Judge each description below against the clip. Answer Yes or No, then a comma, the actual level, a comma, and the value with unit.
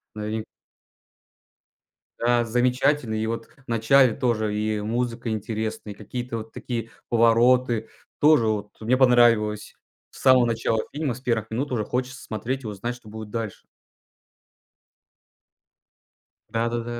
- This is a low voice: Yes, low, 115 Hz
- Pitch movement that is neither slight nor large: No, narrow, 2.2 semitones